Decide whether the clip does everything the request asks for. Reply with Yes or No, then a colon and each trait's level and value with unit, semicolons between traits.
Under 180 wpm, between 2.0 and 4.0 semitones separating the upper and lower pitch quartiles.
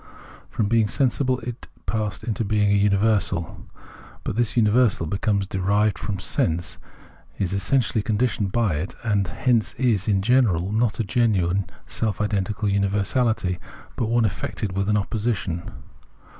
Yes: average, 140 wpm; average, 2.9 semitones